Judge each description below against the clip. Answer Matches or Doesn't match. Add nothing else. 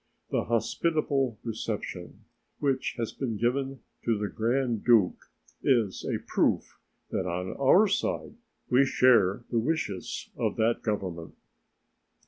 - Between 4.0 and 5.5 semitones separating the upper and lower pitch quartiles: Matches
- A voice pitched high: Doesn't match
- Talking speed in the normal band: Doesn't match